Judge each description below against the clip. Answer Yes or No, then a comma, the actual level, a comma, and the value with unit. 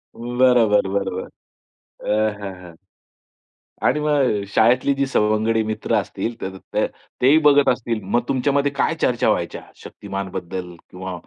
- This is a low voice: Yes, low, 115 Hz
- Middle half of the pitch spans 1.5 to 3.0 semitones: No, average, 5.1 semitones